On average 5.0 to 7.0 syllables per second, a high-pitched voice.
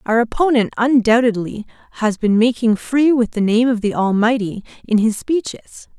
No: 4.8 syllables/s; high, 230 Hz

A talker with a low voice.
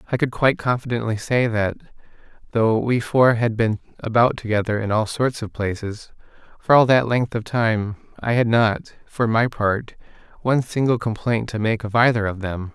Yes: low, 115 Hz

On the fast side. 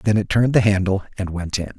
Yes: fast, 270 wpm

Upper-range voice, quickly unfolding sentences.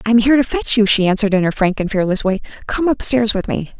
Yes: high, 215 Hz; fast, 285 wpm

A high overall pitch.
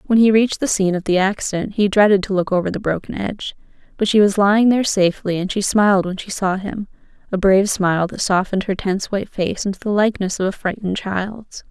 Yes: high, 195 Hz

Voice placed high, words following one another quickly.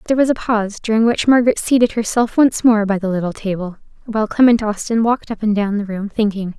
Yes: high, 215 Hz; fast, 230 wpm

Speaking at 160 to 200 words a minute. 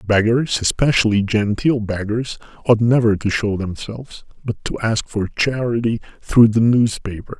No: average, 140 wpm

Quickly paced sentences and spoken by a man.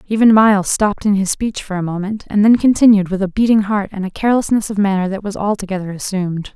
No: fast, 230 wpm; female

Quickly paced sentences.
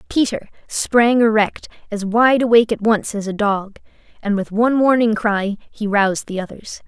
No: average, 175 wpm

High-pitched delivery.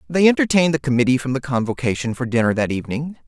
No: medium, 140 Hz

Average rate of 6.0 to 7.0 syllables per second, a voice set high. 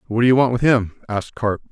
No: 6.8 syllables/s; low, 115 Hz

